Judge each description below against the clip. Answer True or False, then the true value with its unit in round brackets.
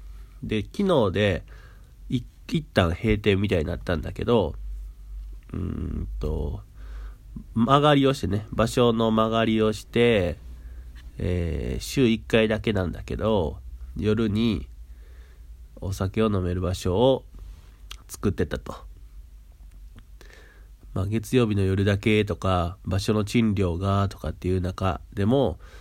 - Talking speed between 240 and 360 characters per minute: False (215 characters per minute)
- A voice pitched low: True (95 Hz)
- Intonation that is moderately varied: False (6.2 semitones)